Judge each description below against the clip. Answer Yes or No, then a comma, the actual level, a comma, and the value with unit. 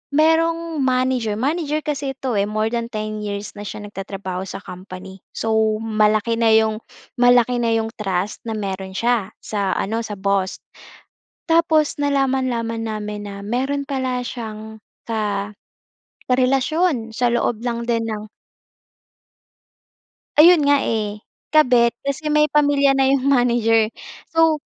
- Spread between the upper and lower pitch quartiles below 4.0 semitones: No, average, 4.3 semitones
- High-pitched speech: Yes, high, 235 Hz